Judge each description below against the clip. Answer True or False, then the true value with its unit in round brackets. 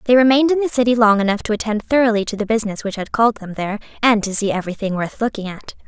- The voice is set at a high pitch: True (220 Hz)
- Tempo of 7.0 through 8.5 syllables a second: True (7.4 syllables/s)